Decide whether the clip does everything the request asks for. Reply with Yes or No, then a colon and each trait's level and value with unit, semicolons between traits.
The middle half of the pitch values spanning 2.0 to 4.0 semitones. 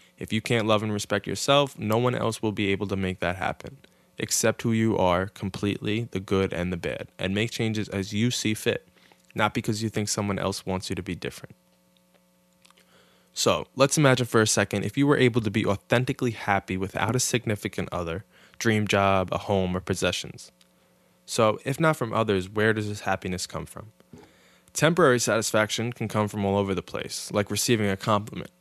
Yes: average, 3.2 semitones